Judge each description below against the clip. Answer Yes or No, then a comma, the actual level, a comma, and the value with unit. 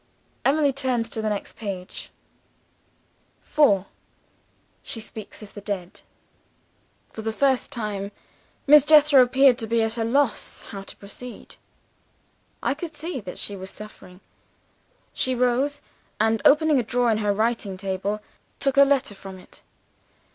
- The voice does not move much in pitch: No, average, 5.0 semitones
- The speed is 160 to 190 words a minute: No, average, 145 wpm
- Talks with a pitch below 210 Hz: No, high, 230 Hz